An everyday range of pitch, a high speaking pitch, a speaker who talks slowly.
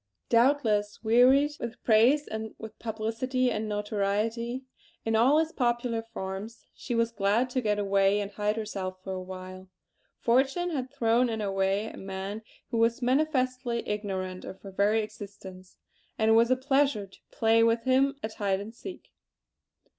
No: average, 3.6 semitones; high, 225 Hz; average, 165 wpm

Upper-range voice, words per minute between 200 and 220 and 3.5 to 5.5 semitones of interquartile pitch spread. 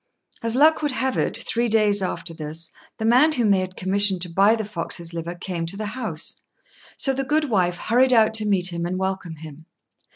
Yes: high, 200 Hz; fast, 205 wpm; average, 4.9 semitones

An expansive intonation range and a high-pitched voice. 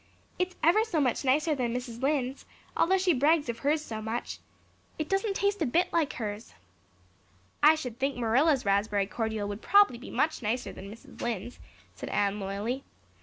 Yes: wide, 6.0 semitones; very high, 255 Hz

